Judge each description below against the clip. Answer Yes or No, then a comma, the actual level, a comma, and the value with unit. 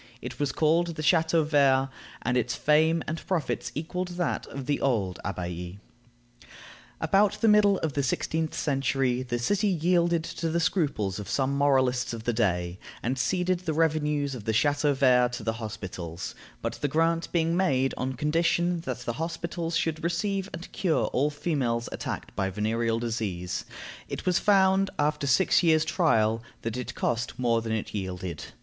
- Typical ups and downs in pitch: No, wide, 6.1 semitones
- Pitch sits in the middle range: Yes, medium, 145 Hz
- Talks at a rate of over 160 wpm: Yes, average, 170 wpm